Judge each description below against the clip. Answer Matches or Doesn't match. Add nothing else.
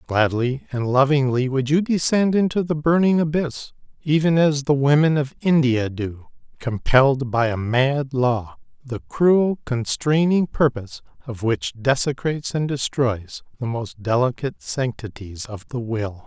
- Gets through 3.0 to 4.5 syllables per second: Matches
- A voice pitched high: Doesn't match